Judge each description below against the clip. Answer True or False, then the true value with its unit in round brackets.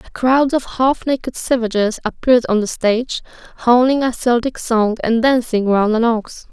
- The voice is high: True (235 Hz)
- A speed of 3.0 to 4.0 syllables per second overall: False (4.8 syllables/s)